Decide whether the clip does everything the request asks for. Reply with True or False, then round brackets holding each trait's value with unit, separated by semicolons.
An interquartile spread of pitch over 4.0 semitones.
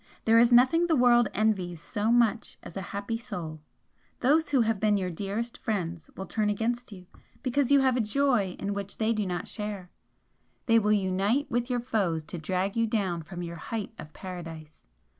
True (4.5 semitones)